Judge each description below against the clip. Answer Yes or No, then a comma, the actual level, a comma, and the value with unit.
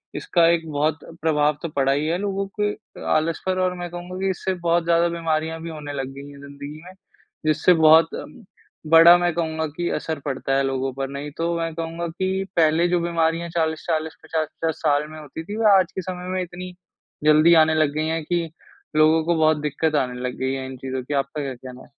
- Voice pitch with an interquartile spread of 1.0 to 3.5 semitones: Yes, average, 2.8 semitones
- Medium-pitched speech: Yes, medium, 160 Hz